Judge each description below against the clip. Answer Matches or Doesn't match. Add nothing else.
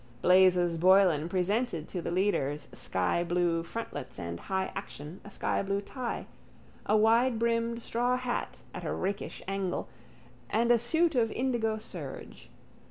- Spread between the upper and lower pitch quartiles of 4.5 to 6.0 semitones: Matches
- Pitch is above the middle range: Matches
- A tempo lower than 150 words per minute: Matches